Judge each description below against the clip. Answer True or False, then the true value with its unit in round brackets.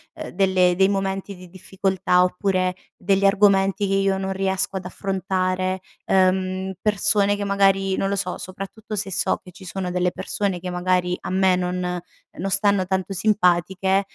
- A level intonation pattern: True (1.2 semitones)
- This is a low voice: False (190 Hz)